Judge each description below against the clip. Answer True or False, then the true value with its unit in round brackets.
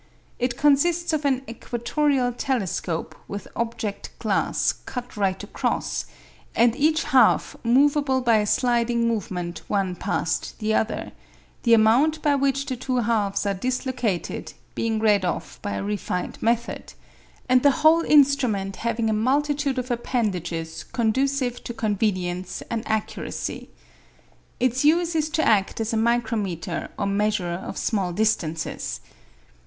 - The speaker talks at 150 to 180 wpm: False (135 wpm)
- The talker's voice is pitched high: True (235 Hz)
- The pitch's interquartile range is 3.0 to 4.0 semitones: False (4.5 semitones)